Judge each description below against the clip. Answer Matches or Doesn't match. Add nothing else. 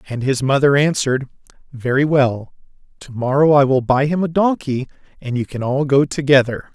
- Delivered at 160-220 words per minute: Matches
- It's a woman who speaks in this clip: Doesn't match